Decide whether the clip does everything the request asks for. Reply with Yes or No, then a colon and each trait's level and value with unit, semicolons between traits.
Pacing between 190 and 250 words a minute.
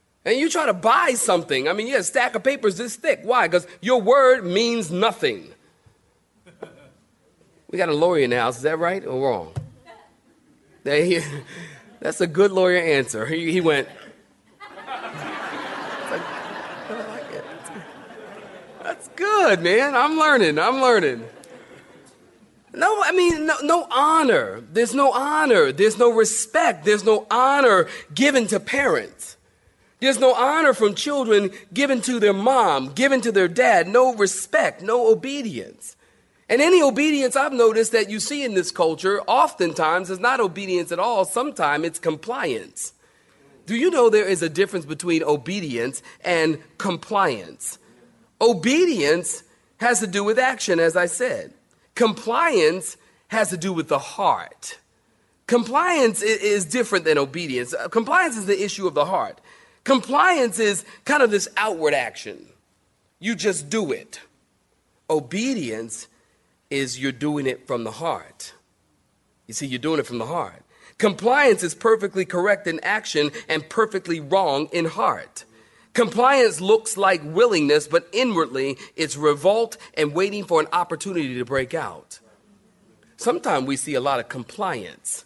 No: average, 145 wpm